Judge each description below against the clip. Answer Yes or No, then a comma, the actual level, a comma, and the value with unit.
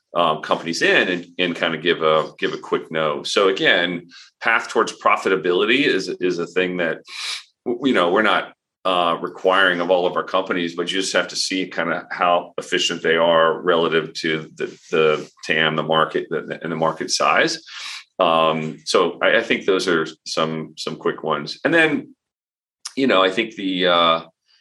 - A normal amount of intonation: No, narrow, 2.3 semitones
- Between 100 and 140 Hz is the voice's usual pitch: No, very low, 85 Hz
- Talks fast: No, average, 190 wpm